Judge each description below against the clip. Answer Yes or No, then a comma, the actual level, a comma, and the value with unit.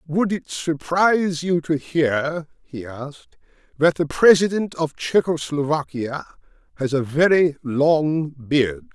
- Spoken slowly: Yes, slow, 125 wpm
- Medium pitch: Yes, medium, 150 Hz